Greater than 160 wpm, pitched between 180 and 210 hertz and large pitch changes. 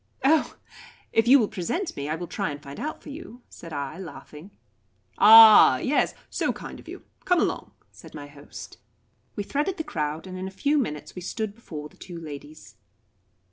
Yes: average, 190 wpm; medium, 185 Hz; wide, 8.3 semitones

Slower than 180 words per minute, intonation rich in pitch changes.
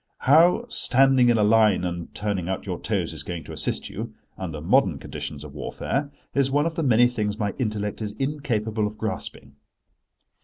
No: average, 185 wpm; wide, 5.9 semitones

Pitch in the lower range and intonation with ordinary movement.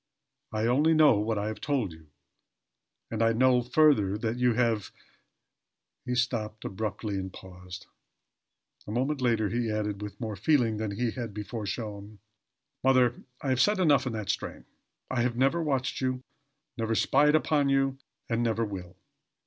Yes: low, 115 Hz; average, 3.7 semitones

